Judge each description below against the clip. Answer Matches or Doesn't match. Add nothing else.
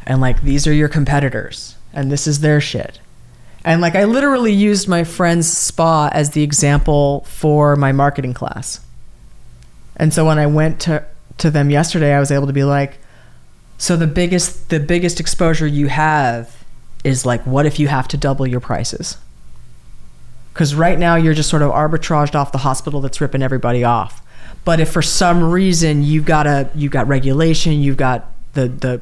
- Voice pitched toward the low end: Doesn't match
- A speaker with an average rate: Matches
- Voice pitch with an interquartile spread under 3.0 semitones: Doesn't match